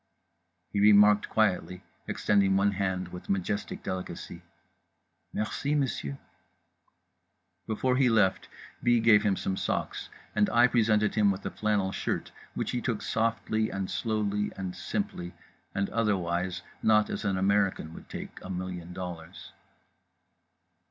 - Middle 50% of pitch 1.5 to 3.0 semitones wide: Yes, average, 2.7 semitones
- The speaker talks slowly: Yes, slow, 130 wpm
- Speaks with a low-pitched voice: Yes, low, 100 Hz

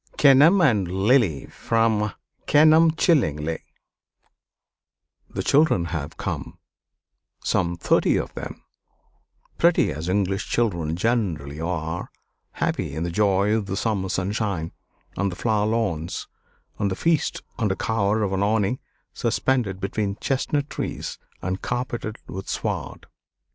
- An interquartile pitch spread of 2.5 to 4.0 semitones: No, average, 4.6 semitones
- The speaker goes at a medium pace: No, slow, 120 wpm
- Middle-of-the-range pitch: No, low, 100 Hz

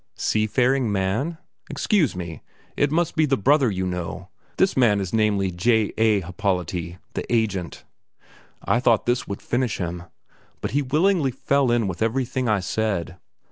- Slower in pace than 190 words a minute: Yes, average, 160 wpm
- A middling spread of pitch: No, wide, 5.7 semitones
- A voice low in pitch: Yes, low, 110 Hz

